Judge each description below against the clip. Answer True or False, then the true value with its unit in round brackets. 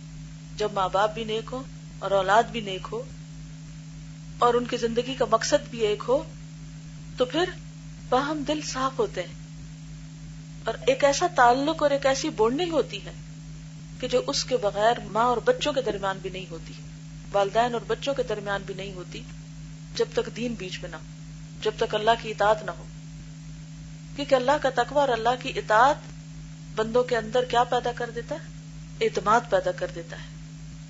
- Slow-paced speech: False (180 wpm)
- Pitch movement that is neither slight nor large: False (7.3 semitones)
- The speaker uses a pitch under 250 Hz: True (190 Hz)